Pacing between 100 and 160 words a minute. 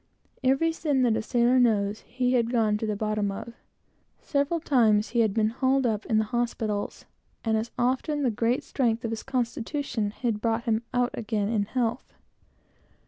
No: average, 180 wpm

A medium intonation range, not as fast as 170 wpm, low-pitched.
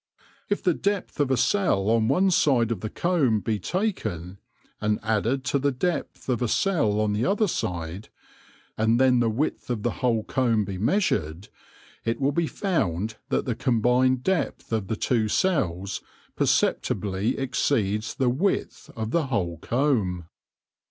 Yes: average, 5.0 semitones; average, 160 wpm; low, 120 Hz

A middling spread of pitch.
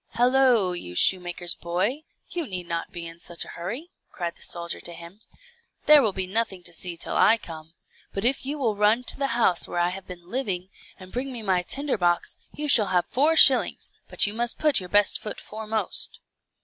No: wide, 5.7 semitones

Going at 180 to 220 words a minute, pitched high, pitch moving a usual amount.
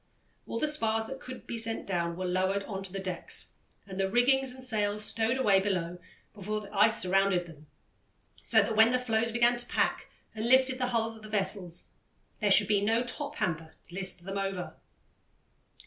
Yes: average, 195 wpm; high, 210 Hz; average, 3.6 semitones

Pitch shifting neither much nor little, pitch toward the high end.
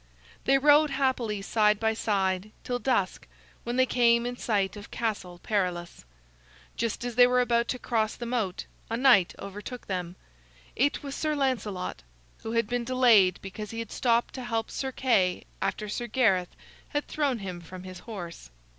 Yes: average, 4.2 semitones; high, 225 Hz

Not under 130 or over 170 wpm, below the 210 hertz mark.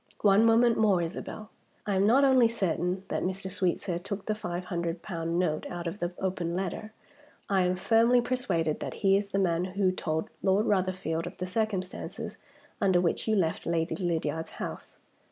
No: average, 180 wpm; medium, 185 Hz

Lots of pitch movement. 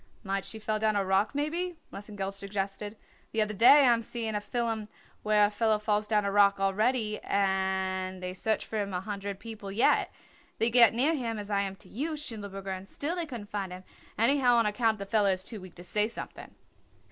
No: average, 2.7 semitones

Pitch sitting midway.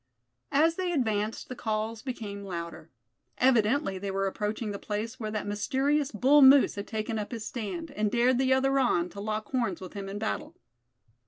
No: high, 220 Hz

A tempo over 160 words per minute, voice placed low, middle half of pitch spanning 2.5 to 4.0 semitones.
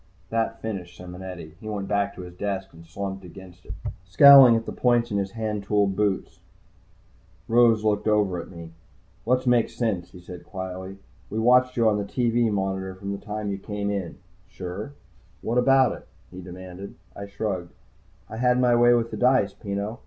Yes: average, 190 wpm; low, 100 Hz; average, 3.4 semitones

